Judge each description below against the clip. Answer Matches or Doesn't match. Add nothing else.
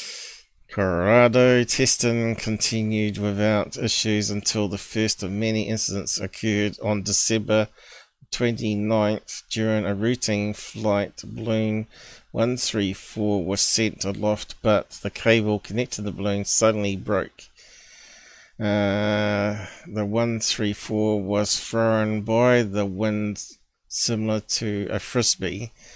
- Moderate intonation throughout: Doesn't match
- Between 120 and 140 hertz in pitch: Doesn't match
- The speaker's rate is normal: Doesn't match